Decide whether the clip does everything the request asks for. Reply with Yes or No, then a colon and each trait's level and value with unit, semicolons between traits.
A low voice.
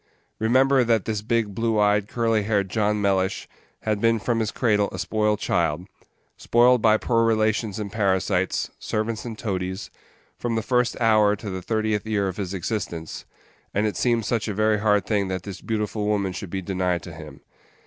Yes: low, 105 Hz